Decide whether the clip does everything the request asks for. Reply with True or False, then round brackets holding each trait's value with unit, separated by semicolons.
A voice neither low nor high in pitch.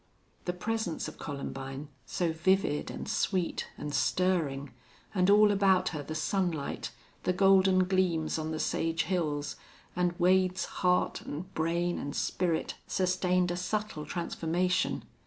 True (180 Hz)